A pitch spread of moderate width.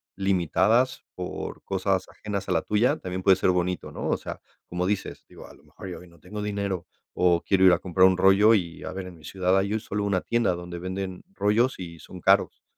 No: narrow, 2.0 semitones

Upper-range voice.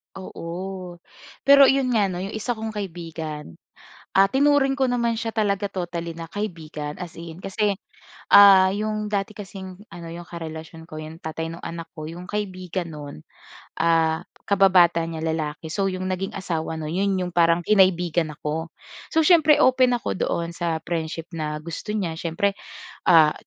No: medium, 180 Hz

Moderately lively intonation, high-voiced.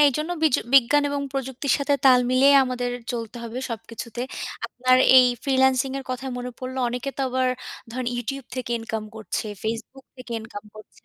No: narrow, 2.2 semitones; very high, 255 Hz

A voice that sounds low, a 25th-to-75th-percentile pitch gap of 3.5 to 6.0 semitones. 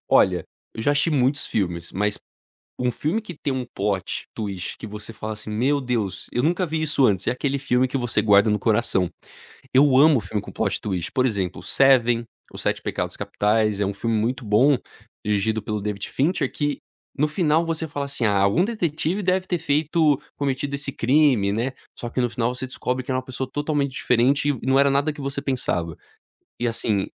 Yes: low, 130 Hz; average, 5.1 semitones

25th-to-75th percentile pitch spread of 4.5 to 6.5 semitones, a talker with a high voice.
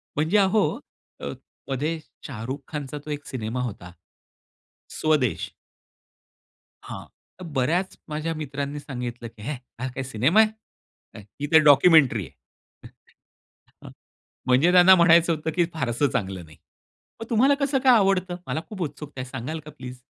No: average, 5.3 semitones; medium, 145 Hz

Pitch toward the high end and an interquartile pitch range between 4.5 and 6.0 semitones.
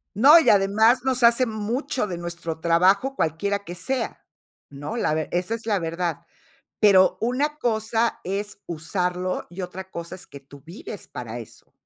Yes: high, 195 Hz; average, 5.0 semitones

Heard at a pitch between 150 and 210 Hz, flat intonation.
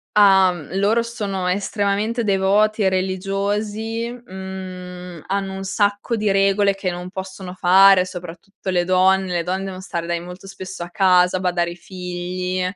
Yes: high, 190 Hz; narrow, 1.7 semitones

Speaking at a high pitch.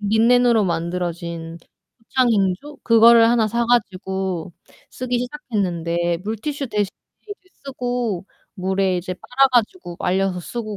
Yes: high, 210 Hz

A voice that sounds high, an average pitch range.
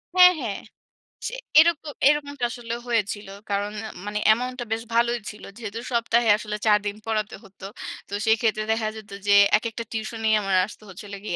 No: high, 220 Hz; narrow, 2.2 semitones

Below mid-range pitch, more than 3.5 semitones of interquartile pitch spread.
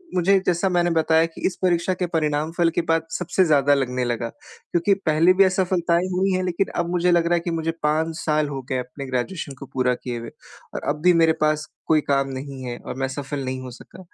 No: medium, 160 Hz; average, 4.1 semitones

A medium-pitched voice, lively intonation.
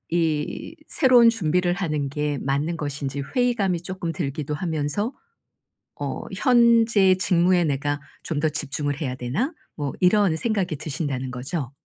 No: medium, 160 Hz; average, 4.7 semitones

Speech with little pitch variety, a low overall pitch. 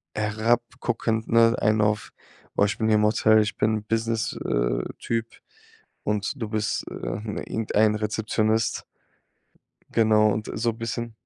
Yes: narrow, 1.1 semitones; low, 110 Hz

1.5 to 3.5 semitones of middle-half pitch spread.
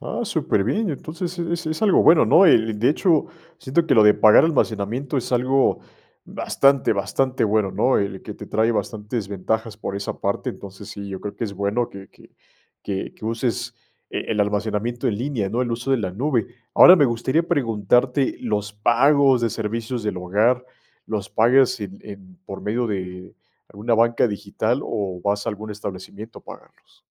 No: average, 4.3 semitones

